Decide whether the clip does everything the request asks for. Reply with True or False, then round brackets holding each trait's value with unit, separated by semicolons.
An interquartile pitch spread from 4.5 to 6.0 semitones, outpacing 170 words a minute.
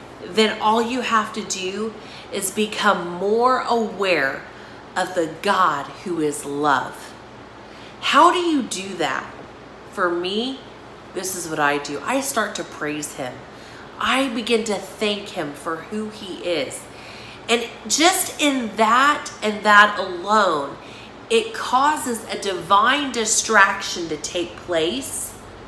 False (4.8 semitones; 135 wpm)